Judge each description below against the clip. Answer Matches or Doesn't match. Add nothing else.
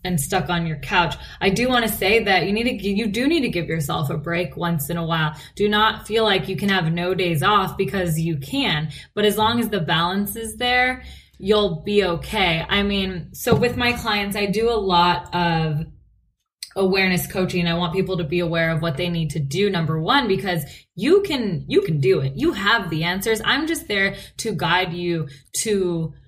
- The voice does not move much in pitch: Doesn't match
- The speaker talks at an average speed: Doesn't match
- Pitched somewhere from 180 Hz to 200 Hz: Matches